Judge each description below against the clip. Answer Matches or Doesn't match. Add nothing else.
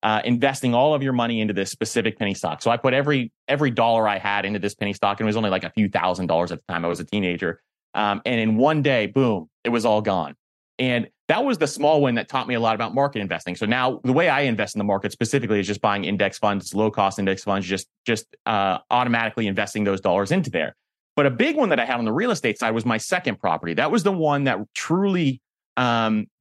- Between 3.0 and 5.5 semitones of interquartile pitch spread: Matches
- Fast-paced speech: Matches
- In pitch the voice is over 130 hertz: Doesn't match